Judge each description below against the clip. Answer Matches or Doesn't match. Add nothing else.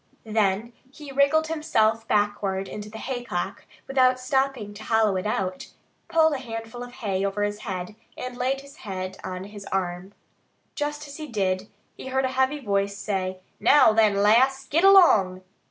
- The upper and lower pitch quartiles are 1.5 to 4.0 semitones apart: Doesn't match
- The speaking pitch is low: Doesn't match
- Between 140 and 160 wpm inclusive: Doesn't match